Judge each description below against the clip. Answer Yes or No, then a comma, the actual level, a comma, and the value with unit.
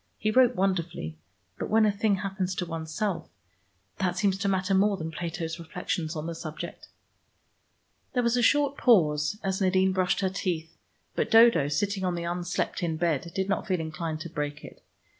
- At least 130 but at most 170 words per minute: No, average, 180 wpm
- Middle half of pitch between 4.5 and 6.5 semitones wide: No, average, 3.5 semitones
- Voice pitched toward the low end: No, medium, 180 Hz